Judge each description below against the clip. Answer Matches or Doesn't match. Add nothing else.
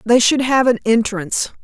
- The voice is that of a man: Doesn't match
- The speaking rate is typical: Matches